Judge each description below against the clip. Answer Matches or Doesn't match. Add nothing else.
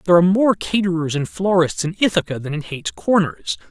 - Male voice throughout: Matches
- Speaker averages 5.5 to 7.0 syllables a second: Matches